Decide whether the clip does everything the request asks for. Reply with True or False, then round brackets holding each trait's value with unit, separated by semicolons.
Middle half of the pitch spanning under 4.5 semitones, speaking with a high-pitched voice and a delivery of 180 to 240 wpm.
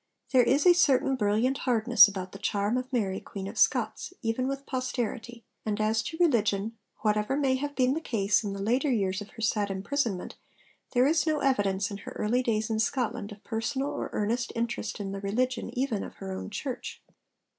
True (4.0 semitones; 225 Hz; 200 wpm)